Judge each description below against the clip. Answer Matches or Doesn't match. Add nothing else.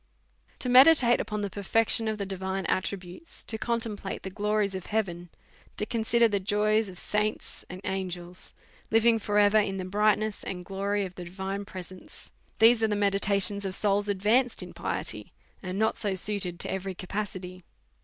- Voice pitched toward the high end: Matches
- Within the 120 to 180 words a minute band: Matches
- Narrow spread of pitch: Matches